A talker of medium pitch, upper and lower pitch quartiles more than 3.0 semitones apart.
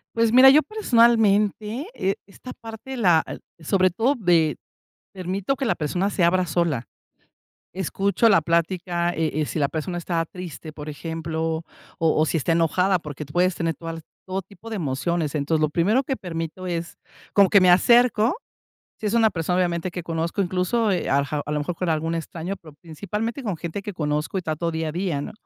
Yes: medium, 175 Hz; average, 3.8 semitones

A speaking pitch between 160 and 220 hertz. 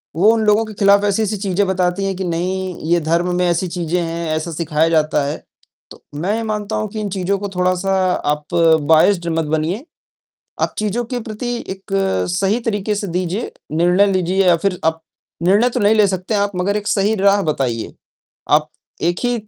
Yes: high, 190 Hz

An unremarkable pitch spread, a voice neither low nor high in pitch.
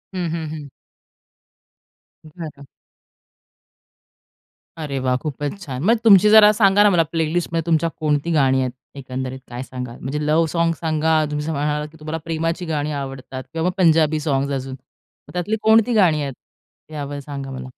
Yes: average, 3.4 semitones; medium, 155 Hz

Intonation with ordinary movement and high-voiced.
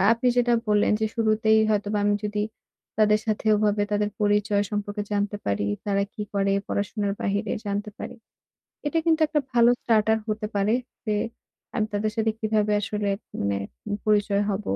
No: narrow, 1.1 semitones; high, 210 Hz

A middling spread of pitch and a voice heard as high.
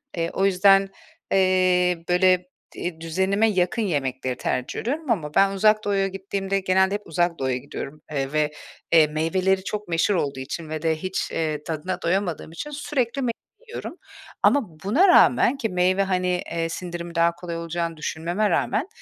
No: average, 3.1 semitones; medium, 180 Hz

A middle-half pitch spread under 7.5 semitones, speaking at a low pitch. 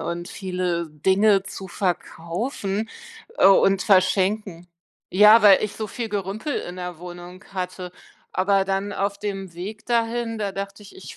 No: narrow, 2.5 semitones; high, 195 Hz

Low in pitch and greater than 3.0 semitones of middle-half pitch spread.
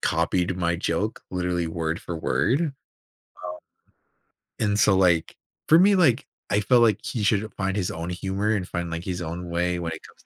Yes: very low, 90 Hz; average, 3.6 semitones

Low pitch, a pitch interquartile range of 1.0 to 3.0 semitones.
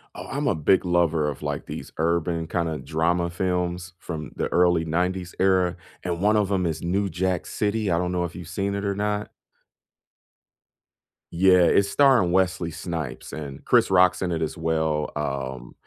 Yes: very low, 90 Hz; narrow, 2.5 semitones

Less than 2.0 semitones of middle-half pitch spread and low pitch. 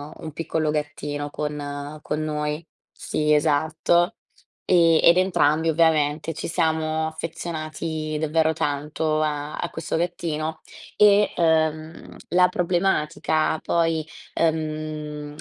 No: narrow, 1.5 semitones; medium, 155 Hz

